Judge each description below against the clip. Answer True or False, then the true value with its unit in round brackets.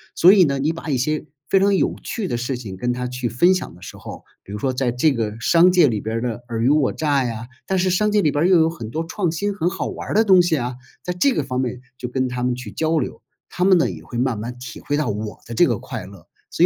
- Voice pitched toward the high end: False (135 Hz)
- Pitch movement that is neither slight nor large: False (6.4 semitones)